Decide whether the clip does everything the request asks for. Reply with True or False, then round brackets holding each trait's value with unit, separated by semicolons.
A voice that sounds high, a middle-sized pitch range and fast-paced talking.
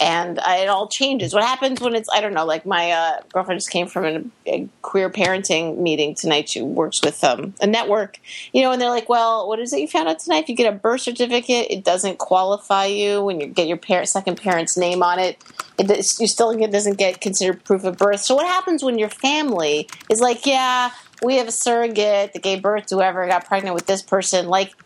True (200 Hz; 4.3 semitones; 240 wpm)